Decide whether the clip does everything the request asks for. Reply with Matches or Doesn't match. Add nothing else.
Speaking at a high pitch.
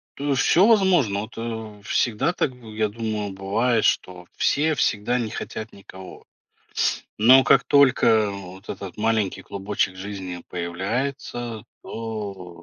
Doesn't match